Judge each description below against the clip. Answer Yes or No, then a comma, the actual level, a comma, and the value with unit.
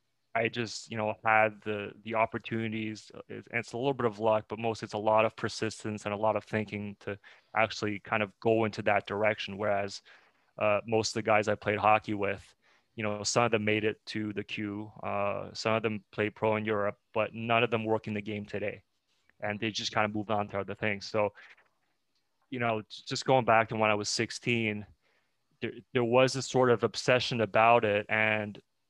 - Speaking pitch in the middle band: No, low, 110 Hz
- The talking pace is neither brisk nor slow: No, fast, 215 wpm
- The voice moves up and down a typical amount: No, narrow, 1.5 semitones